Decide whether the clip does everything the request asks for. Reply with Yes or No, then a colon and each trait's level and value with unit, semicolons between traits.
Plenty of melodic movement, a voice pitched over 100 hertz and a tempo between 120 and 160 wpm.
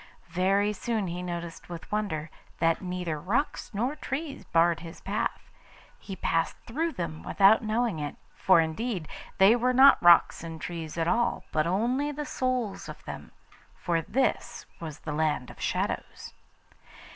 Yes: wide, 6.2 semitones; medium, 185 Hz; average, 155 wpm